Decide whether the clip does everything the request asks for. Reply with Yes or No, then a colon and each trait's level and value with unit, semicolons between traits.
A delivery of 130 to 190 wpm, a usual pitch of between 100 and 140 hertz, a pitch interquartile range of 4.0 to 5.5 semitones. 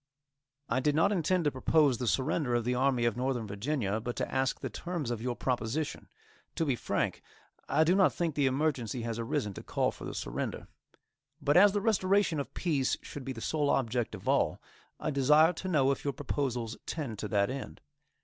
No: fast, 205 wpm; low, 135 Hz; average, 4.6 semitones